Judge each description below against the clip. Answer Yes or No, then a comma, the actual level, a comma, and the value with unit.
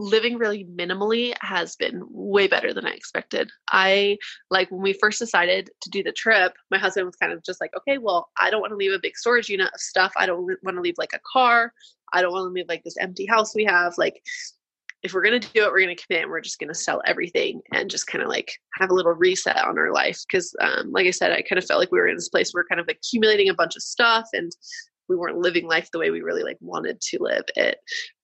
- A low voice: No, high, 210 Hz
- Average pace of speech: No, fast, 265 wpm